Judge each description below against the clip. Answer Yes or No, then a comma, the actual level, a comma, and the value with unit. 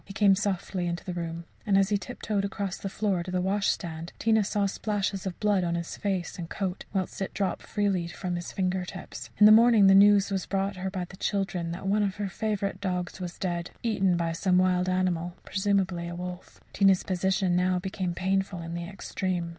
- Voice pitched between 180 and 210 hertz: Yes, high, 190 Hz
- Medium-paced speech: No, fast, 210 wpm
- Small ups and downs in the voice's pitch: Yes, narrow, 1.9 semitones